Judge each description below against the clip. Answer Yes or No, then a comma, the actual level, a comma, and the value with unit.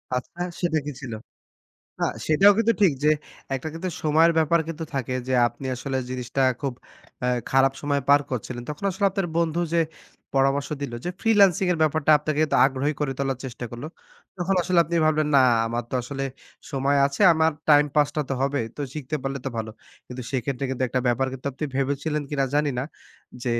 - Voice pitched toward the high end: No, medium, 145 Hz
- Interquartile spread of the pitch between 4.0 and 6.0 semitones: No, average, 3.2 semitones